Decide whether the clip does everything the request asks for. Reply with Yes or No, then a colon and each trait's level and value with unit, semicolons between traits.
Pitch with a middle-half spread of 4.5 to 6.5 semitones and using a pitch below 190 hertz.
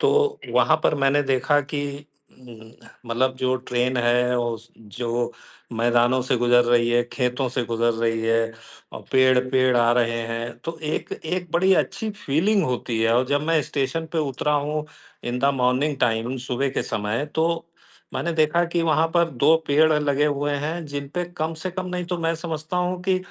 Yes: average, 4.9 semitones; low, 135 Hz